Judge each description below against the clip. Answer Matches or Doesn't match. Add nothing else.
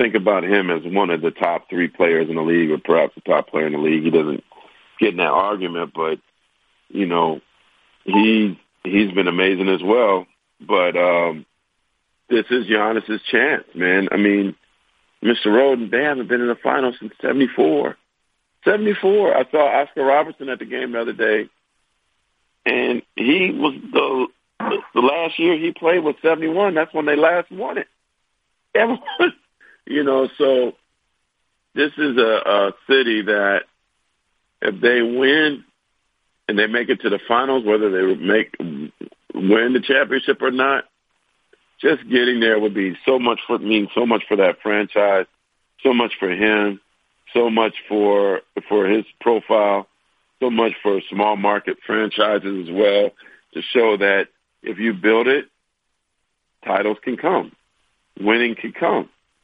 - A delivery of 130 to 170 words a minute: Matches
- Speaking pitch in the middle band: Doesn't match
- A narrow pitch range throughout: Doesn't match